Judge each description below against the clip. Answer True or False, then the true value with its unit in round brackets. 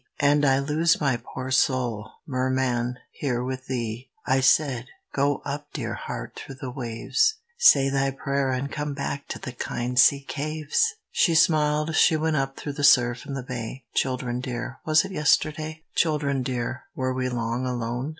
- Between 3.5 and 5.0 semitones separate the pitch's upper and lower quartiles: False (2.8 semitones)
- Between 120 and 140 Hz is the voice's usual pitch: True (135 Hz)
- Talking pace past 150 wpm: True (170 wpm)